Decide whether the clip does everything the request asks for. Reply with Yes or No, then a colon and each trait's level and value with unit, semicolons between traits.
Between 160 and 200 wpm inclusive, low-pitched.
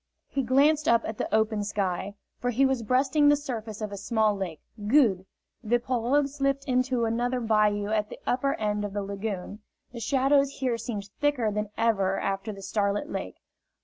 No: average, 180 wpm; high, 225 Hz